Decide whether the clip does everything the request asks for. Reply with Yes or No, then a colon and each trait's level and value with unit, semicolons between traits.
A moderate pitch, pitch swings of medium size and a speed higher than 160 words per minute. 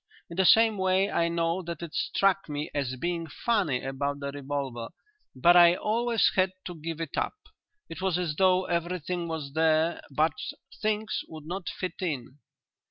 Yes: medium, 170 Hz; average, 4.0 semitones; average, 170 wpm